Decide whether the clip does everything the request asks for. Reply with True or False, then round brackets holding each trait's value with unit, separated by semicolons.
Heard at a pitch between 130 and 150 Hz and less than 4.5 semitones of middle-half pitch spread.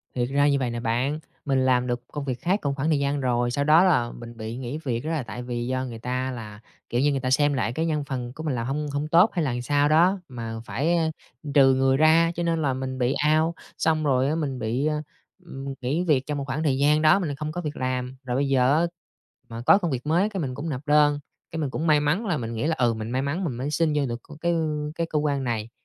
True (140 Hz; 3.6 semitones)